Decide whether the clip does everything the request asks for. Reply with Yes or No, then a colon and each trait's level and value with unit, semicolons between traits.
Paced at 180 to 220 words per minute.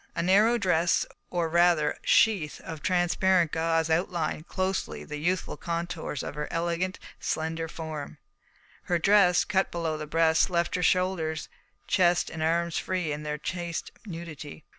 No: average, 145 wpm